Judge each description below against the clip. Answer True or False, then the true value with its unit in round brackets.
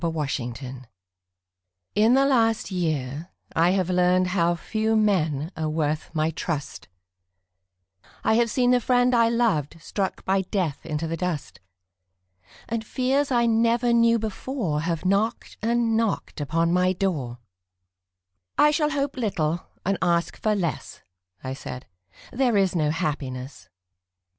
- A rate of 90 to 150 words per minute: True (140 wpm)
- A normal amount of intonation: False (6.8 semitones)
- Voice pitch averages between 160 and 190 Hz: True (185 Hz)